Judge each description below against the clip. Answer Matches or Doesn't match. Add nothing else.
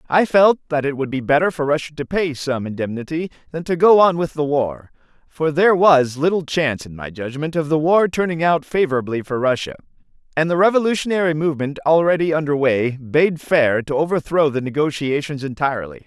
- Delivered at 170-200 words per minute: Matches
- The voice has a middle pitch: Matches